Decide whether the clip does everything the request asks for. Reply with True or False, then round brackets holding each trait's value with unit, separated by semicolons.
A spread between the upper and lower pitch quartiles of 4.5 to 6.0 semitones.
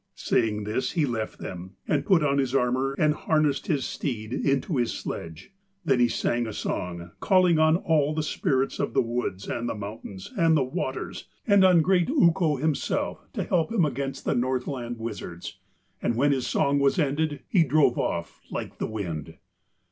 True (5.2 semitones)